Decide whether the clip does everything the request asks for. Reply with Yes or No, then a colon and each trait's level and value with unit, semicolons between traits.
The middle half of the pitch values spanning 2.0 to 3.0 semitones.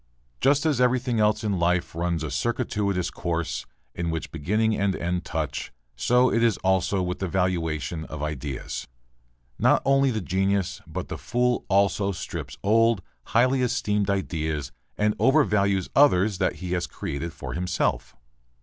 No: average, 4.7 semitones